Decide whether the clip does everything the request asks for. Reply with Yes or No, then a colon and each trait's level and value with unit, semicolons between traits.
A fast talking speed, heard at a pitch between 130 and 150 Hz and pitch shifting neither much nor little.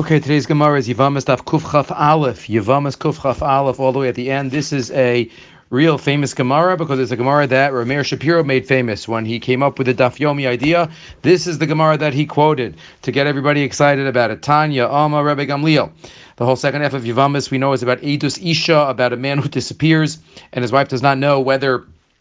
No: fast, 220 wpm; medium, 140 Hz; narrow, 2.3 semitones